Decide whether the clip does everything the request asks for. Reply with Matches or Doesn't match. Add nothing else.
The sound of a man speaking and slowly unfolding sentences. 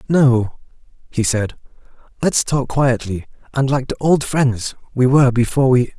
Doesn't match